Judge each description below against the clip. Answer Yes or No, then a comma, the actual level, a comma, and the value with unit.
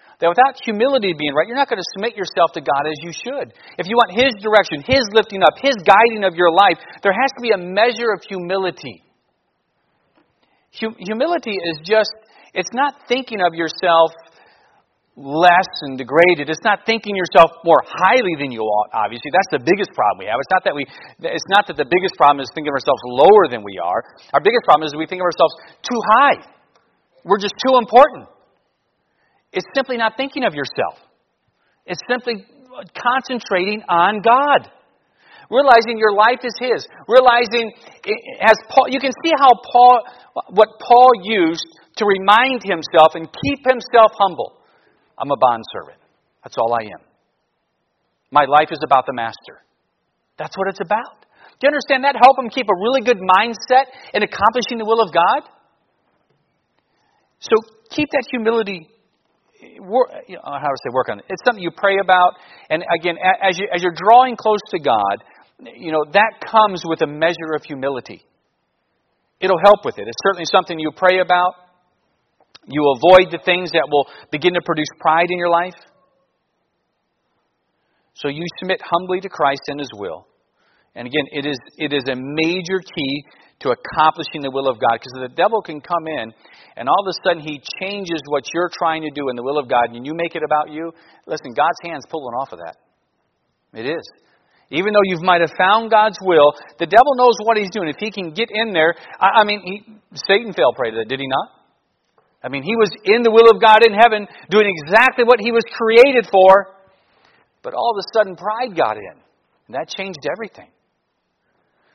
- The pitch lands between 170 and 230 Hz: Yes, high, 190 Hz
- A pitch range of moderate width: No, wide, 6.0 semitones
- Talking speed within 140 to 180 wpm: No, average, 190 wpm